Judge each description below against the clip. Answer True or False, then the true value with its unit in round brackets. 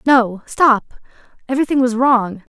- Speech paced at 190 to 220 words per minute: False (120 wpm)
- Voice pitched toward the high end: True (245 Hz)